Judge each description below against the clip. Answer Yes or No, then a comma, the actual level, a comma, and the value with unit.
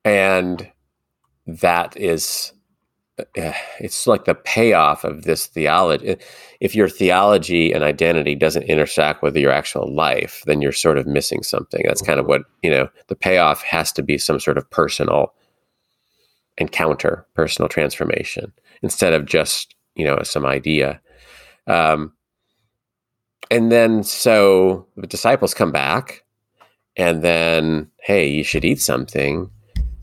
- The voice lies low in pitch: Yes, very low, 85 Hz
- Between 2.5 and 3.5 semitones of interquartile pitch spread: No, average, 4.9 semitones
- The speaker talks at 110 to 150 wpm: Yes, slow, 135 wpm